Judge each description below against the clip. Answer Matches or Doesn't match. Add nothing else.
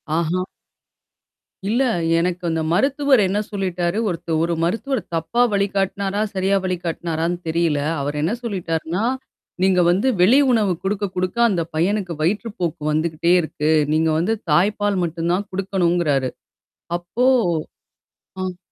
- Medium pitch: Matches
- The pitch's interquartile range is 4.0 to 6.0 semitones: Doesn't match